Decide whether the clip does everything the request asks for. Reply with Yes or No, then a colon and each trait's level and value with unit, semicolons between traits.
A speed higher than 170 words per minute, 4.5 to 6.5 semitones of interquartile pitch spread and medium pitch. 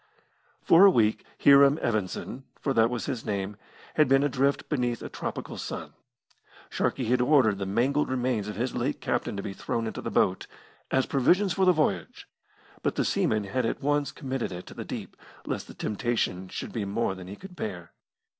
No: average, 190 wpm; average, 5.1 semitones; low, 120 Hz